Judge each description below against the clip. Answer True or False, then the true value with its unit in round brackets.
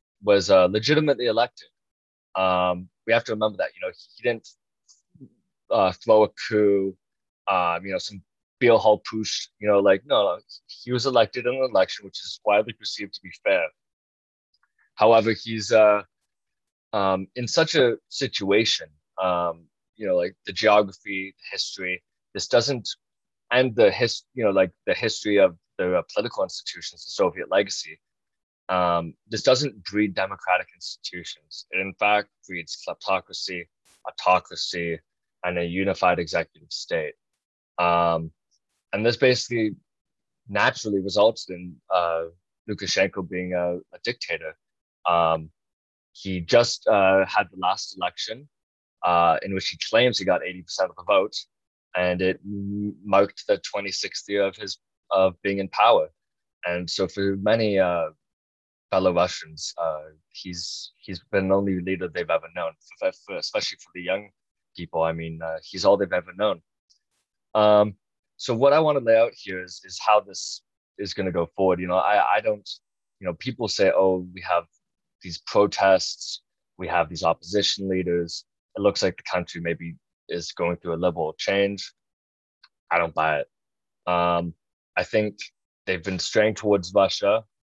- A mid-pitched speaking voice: False (95 Hz)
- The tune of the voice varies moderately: True (3.2 semitones)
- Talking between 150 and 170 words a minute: True (160 wpm)